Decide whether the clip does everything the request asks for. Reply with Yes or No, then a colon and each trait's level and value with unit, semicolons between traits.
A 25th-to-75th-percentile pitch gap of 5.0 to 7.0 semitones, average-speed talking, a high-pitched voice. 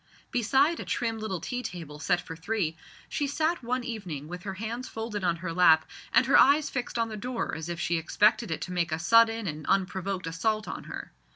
No: wide, 5.5 semitones; fast, 215 wpm; high, 205 Hz